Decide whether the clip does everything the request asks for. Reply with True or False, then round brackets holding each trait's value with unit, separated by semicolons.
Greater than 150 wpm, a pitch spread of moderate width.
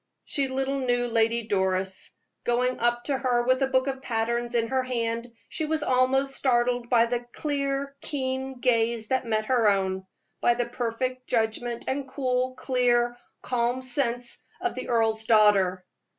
False (160 wpm; 2.1 semitones)